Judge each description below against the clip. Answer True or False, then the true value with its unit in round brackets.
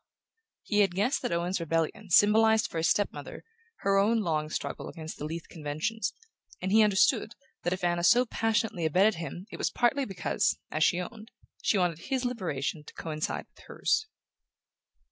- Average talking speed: True (175 wpm)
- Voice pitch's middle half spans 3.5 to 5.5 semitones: True (4.9 semitones)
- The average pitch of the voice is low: False (190 Hz)